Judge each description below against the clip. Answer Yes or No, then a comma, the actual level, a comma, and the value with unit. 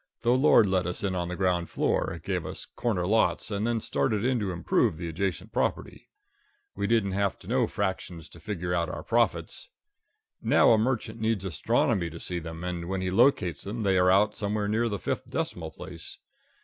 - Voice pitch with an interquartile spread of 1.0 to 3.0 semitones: No, average, 3.6 semitones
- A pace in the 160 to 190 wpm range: No, average, 200 wpm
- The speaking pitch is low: Yes, very low, 95 Hz